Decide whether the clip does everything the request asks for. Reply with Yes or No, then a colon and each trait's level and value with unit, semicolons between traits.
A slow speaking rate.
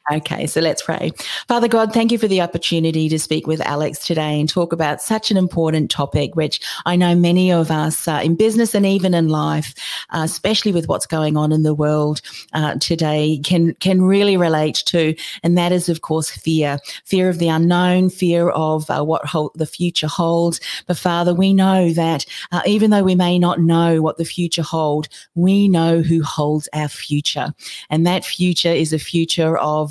No: average, 195 wpm